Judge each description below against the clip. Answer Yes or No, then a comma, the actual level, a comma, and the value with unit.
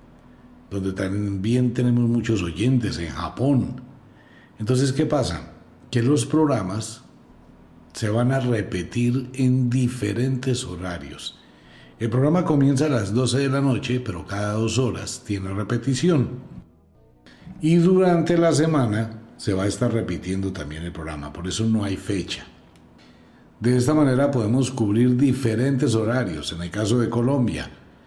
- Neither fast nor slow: Yes, average, 135 wpm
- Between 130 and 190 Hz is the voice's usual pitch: No, low, 120 Hz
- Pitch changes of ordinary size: Yes, average, 4.9 semitones